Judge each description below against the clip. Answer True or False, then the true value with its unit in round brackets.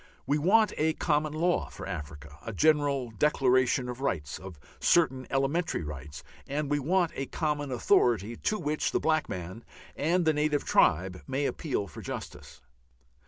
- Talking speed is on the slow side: False (160 wpm)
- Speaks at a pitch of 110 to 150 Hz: True (140 Hz)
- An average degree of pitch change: False (7.1 semitones)